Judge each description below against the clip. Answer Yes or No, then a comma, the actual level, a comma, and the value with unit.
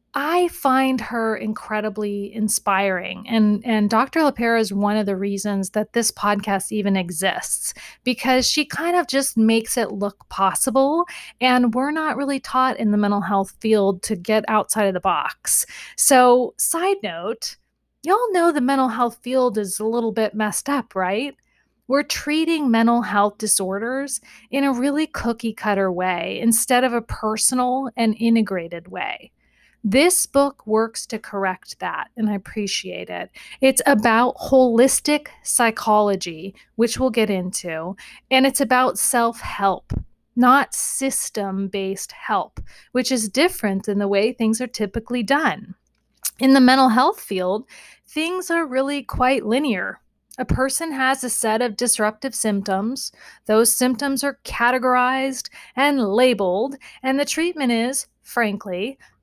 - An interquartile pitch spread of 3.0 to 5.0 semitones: Yes, average, 4.2 semitones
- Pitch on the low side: No, high, 235 Hz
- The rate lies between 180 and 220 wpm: No, average, 145 wpm